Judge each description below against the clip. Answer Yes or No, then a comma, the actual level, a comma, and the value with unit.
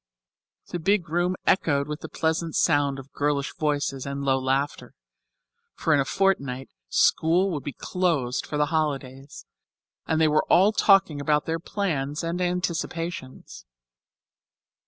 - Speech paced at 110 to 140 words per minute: Yes, slow, 135 wpm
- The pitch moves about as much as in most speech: Yes, average, 3.7 semitones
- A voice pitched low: No, medium, 150 Hz